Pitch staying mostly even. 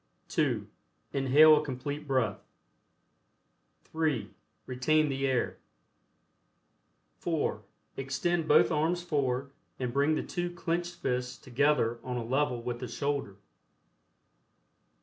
No: average, 3.6 semitones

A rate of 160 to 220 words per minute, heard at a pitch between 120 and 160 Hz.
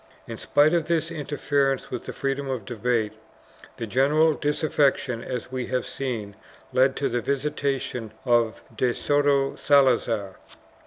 No: average, 145 wpm; low, 135 Hz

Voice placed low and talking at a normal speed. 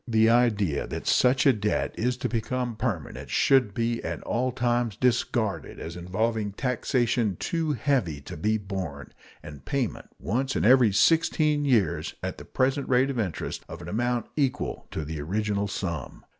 Yes: low, 115 Hz; average, 165 wpm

